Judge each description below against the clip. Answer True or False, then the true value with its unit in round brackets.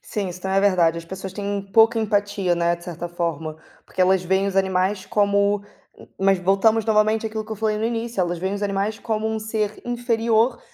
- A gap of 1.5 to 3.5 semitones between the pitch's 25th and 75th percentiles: True (2.8 semitones)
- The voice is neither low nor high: False (200 Hz)